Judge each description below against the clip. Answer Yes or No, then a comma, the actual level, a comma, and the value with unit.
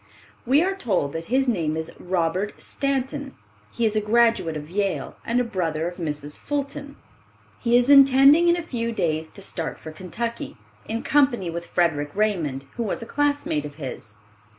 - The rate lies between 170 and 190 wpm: Yes, average, 175 wpm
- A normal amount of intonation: No, wide, 8.4 semitones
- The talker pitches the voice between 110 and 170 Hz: No, high, 210 Hz